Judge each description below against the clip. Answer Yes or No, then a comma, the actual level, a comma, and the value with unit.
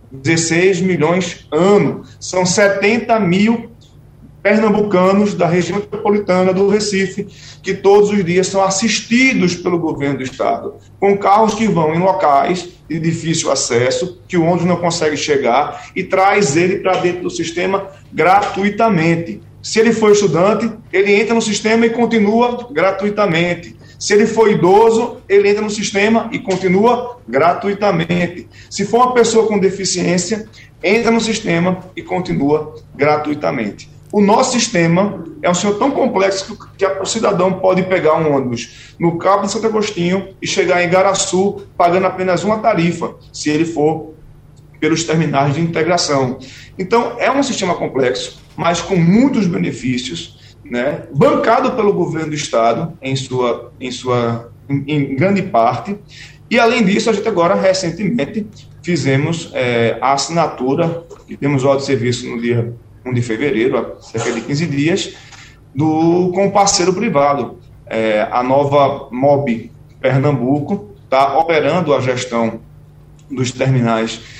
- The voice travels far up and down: Yes, wide, 6.0 semitones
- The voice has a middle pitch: Yes, medium, 175 Hz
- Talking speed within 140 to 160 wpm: Yes, average, 145 wpm